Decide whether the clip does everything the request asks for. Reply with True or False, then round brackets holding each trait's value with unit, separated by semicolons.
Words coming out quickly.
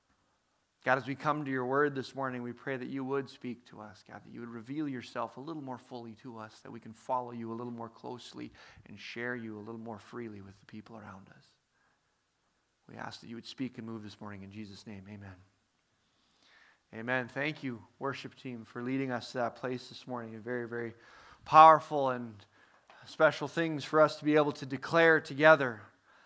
True (210 wpm)